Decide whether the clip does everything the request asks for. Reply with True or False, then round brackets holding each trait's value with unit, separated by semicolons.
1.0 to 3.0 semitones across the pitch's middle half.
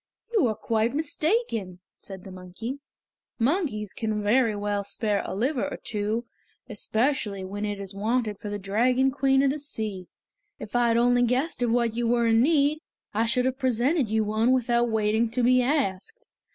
False (3.7 semitones)